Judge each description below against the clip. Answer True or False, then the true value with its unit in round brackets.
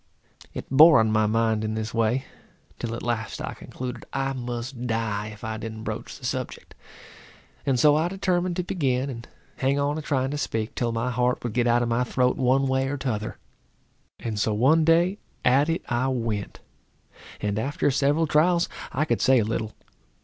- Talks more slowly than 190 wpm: False (195 wpm)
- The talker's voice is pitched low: True (125 Hz)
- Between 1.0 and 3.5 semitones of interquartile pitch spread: False (3.9 semitones)